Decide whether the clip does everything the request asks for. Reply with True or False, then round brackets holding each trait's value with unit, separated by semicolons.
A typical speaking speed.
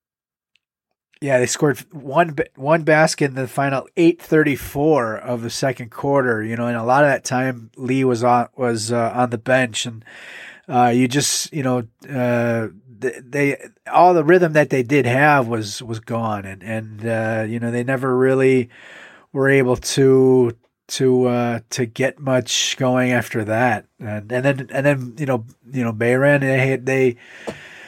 True (170 wpm)